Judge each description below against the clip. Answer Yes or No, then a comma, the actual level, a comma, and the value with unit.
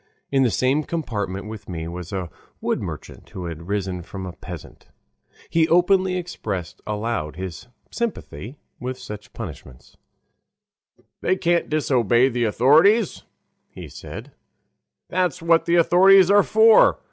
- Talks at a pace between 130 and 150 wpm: Yes, slow, 135 wpm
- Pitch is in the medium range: No, low, 120 Hz